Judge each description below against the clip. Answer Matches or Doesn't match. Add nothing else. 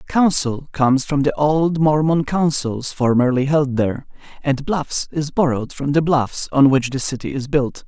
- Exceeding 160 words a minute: Matches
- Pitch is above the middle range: Doesn't match